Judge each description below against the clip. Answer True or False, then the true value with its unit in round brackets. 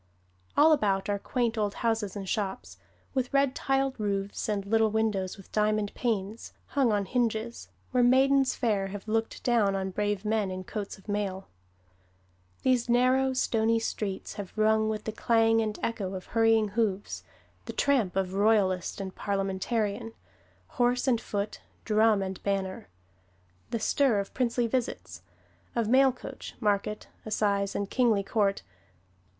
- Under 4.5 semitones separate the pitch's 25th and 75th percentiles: True (3.0 semitones)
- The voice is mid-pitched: False (215 Hz)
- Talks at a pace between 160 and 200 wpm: False (150 wpm)